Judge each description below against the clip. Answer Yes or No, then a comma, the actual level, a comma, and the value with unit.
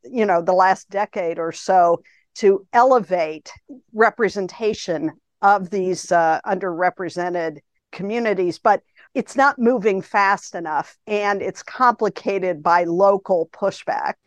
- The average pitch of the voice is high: Yes, high, 195 Hz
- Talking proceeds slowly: Yes, slow, 115 wpm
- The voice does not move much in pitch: No, average, 3.7 semitones